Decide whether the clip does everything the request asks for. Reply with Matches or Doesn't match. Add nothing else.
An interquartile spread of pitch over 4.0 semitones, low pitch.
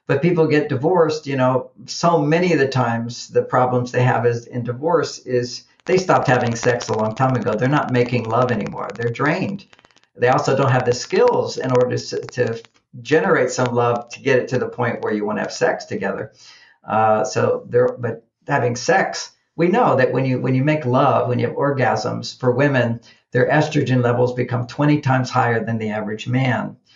Doesn't match